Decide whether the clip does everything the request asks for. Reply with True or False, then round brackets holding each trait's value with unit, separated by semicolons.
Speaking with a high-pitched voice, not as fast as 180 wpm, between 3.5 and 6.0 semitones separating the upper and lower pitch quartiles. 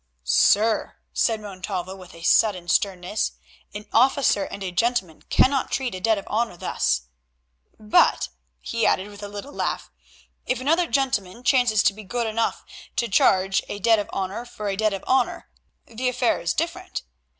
True (215 Hz; 170 wpm; 4.0 semitones)